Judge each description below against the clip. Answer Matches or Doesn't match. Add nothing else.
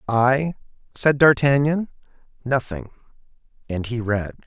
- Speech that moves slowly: Matches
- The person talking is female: Doesn't match